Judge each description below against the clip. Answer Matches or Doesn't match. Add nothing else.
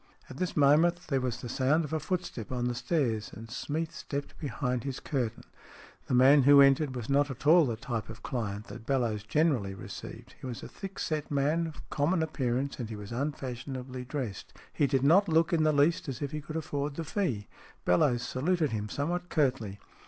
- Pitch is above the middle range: Doesn't match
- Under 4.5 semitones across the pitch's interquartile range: Matches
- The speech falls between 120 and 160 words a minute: Doesn't match